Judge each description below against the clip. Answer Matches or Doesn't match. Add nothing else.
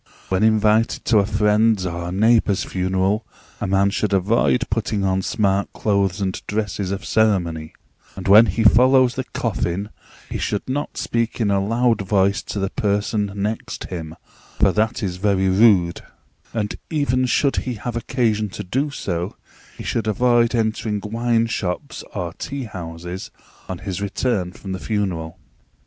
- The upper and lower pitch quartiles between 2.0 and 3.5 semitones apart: Matches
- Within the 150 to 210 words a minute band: Matches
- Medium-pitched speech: Doesn't match